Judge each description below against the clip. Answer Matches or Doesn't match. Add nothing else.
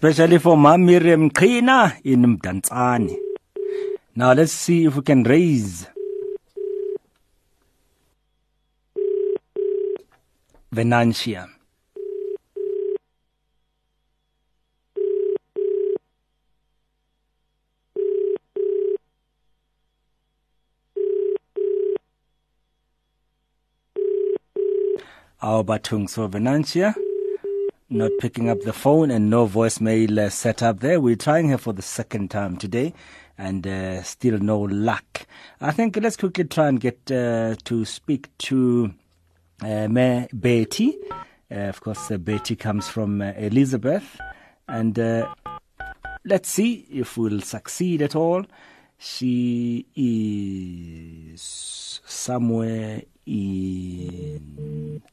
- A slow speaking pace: Matches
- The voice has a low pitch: Matches